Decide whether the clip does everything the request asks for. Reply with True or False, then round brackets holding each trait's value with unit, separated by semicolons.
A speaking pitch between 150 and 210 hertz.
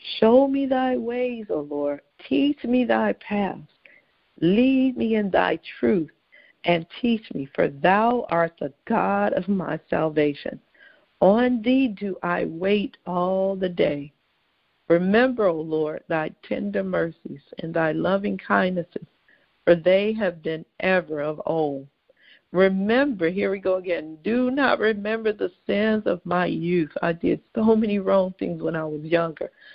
True (190 Hz)